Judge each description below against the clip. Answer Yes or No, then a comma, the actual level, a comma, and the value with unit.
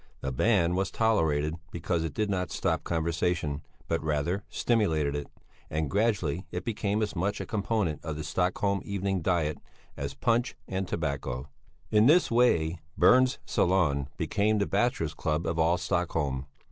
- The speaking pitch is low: Yes, very low, 90 Hz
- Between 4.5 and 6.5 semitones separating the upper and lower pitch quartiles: Yes, average, 4.8 semitones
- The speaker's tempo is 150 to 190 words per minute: Yes, average, 155 wpm